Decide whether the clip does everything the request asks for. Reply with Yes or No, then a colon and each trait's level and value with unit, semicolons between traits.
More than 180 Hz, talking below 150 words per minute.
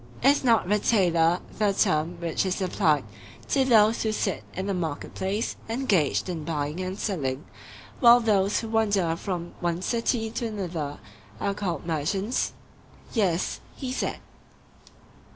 Yes: high, 190 Hz; average, 140 wpm